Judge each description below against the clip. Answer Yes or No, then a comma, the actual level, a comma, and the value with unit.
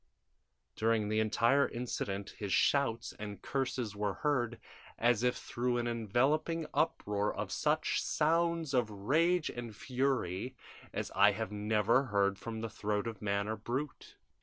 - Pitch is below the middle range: Yes, low, 115 Hz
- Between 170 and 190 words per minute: No, average, 145 wpm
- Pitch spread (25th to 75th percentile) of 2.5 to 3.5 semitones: No, average, 4.1 semitones